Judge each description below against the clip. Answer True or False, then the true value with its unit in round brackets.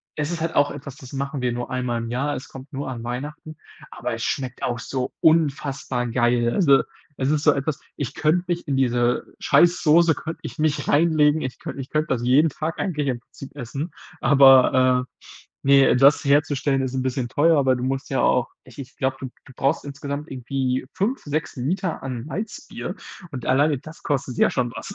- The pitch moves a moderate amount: True (3.1 semitones)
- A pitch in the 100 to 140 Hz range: True (135 Hz)